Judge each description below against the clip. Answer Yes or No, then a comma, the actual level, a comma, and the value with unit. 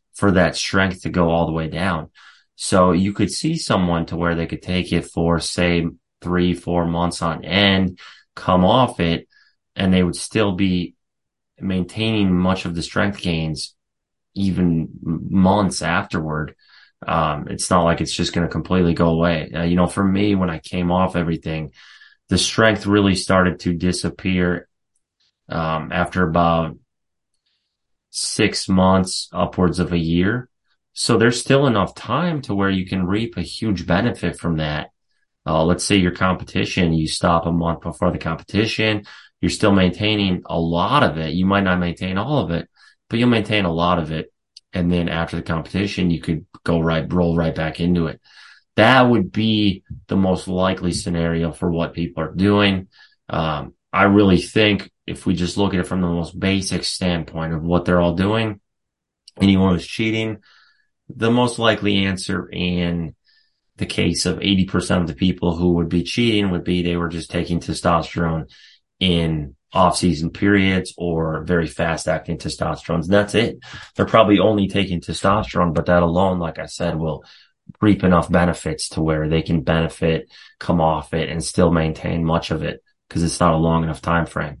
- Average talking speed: No, fast, 175 wpm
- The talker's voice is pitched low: Yes, very low, 90 Hz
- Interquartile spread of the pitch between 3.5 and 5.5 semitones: No, average, 2.7 semitones